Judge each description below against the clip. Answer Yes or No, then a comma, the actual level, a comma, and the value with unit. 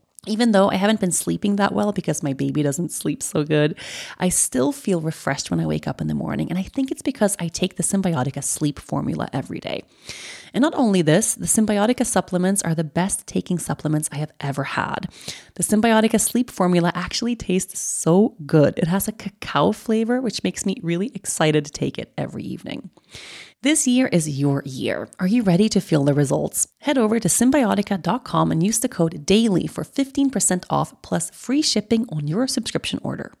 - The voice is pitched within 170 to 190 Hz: Yes, medium, 185 Hz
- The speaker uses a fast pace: No, average, 195 wpm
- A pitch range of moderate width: No, wide, 6.2 semitones